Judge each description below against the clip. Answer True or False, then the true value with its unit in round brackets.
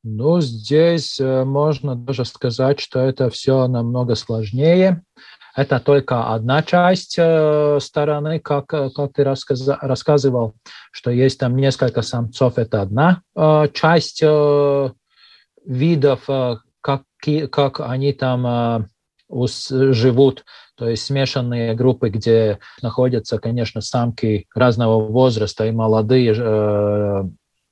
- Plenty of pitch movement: False (3.5 semitones)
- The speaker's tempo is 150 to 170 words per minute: False (115 wpm)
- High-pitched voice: False (130 Hz)